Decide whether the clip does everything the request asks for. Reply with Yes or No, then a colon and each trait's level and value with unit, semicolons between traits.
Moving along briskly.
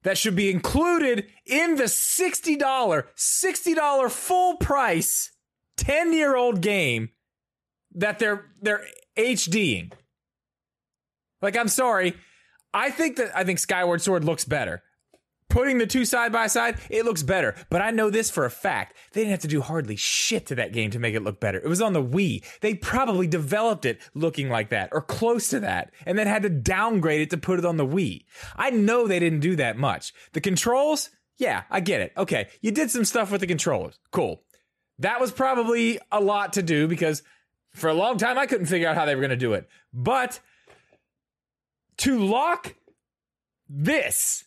No: average, 190 wpm